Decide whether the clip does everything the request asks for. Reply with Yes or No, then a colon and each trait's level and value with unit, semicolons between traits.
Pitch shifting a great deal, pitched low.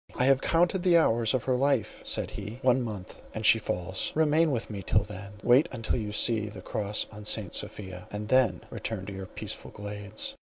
No: average, 4.2 semitones; low, 110 Hz